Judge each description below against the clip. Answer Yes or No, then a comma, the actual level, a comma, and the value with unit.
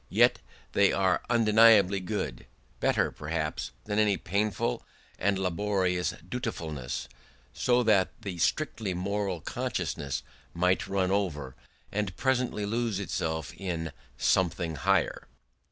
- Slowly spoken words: Yes, slow, 110 wpm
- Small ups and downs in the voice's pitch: No, average, 3.7 semitones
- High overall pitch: No, very low, 95 Hz